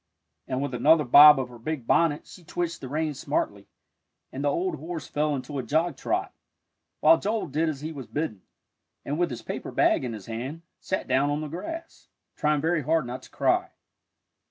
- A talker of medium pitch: Yes, medium, 150 Hz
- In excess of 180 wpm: Yes, average, 200 wpm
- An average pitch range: Yes, average, 3.8 semitones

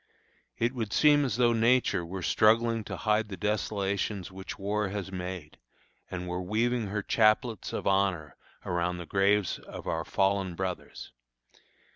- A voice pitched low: Yes, low, 100 Hz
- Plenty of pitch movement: No, average, 3.2 semitones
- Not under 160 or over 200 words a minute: No, average, 150 wpm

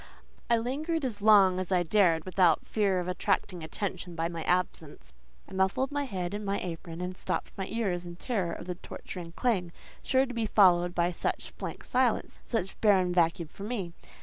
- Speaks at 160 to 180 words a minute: No, average, 190 wpm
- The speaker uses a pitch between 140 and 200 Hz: Yes, medium, 185 Hz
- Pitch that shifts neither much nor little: Yes, average, 3.6 semitones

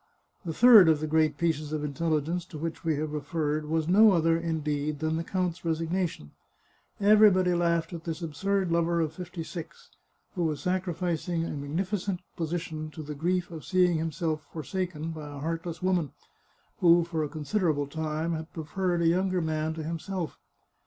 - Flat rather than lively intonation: Yes, narrow, 2.3 semitones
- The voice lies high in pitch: No, medium, 165 Hz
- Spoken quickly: No, average, 175 wpm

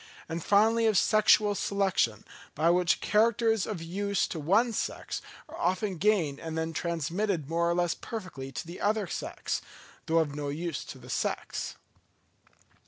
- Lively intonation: No, average, 4.4 semitones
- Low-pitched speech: No, medium, 180 Hz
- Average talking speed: Yes, average, 160 wpm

